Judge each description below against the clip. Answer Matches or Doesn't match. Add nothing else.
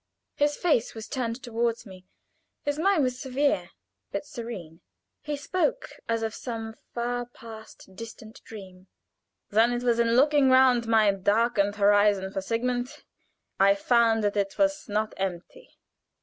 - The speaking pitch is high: Matches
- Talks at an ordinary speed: Matches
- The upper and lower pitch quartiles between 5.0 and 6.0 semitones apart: Doesn't match